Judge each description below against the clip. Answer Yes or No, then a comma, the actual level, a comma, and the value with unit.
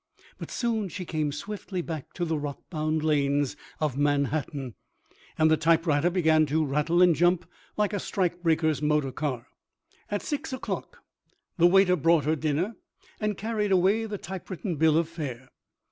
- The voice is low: No, medium, 160 Hz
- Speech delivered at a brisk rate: No, average, 160 wpm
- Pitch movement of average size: Yes, average, 3.8 semitones